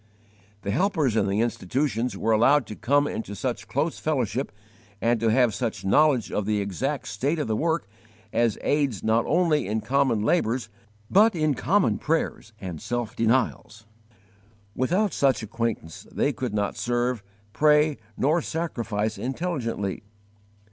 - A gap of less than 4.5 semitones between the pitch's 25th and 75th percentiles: No, wide, 5.4 semitones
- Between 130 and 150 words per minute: Yes, average, 145 wpm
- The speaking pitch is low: Yes, low, 120 Hz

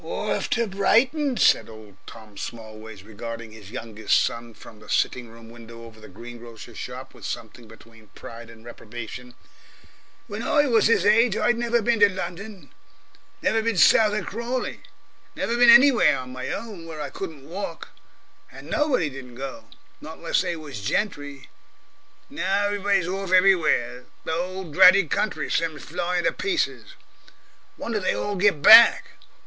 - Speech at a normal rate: Yes, average, 160 wpm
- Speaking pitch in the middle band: Yes, medium, 170 Hz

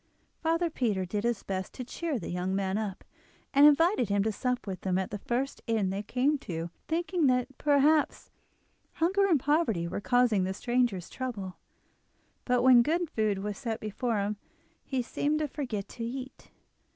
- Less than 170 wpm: No, average, 175 wpm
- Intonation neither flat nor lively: No, wide, 6.1 semitones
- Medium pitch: No, high, 240 Hz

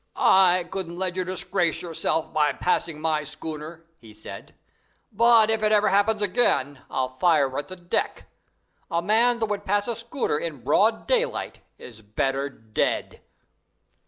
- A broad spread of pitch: Yes, wide, 5.9 semitones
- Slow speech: No, average, 155 wpm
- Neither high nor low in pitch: Yes, medium, 175 Hz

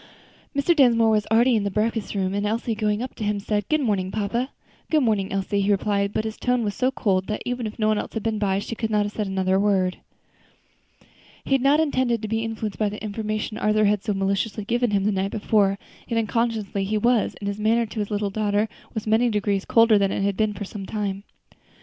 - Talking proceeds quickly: Yes, fast, 235 wpm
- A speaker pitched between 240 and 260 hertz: No, high, 215 Hz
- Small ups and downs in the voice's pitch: Yes, narrow, 2.1 semitones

